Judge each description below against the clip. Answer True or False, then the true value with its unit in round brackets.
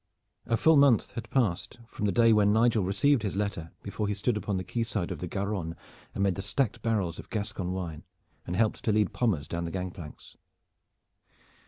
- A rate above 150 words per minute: True (200 wpm)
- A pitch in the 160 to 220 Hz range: False (100 Hz)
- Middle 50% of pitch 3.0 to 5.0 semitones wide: True (3.7 semitones)